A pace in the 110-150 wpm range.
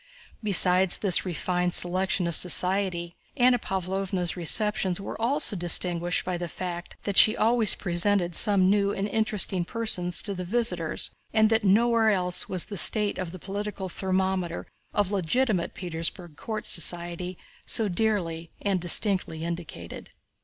Yes: average, 140 wpm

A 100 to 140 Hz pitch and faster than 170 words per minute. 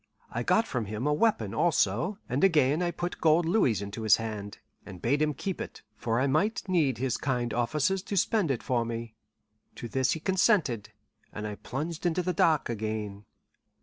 Yes: low, 135 Hz; average, 190 wpm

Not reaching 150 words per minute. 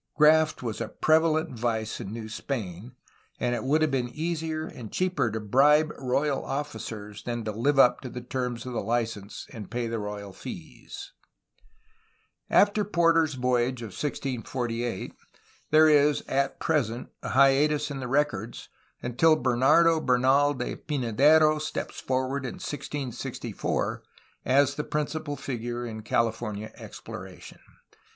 Yes: average, 140 wpm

